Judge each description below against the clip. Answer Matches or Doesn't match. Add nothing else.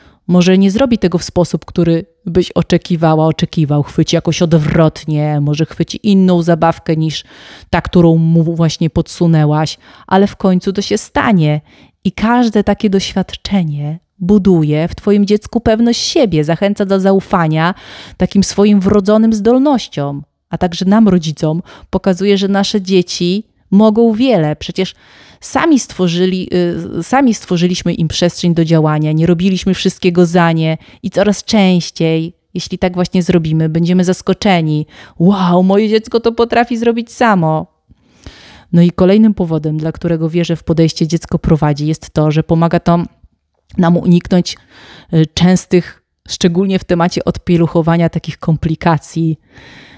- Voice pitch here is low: Doesn't match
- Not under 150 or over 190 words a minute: Doesn't match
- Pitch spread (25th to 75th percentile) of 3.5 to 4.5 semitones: Doesn't match